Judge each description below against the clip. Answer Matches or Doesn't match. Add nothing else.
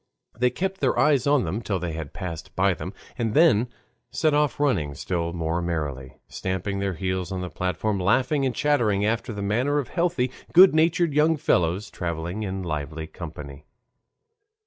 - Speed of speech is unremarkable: Matches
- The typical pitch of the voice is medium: Doesn't match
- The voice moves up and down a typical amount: Doesn't match